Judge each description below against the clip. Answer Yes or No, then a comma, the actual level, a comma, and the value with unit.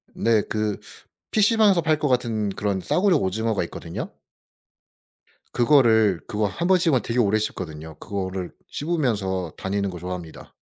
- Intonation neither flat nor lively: No, wide, 7.1 semitones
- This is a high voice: No, low, 110 Hz